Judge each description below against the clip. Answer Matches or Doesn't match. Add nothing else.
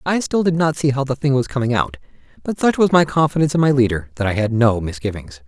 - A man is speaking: Matches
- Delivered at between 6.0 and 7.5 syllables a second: Matches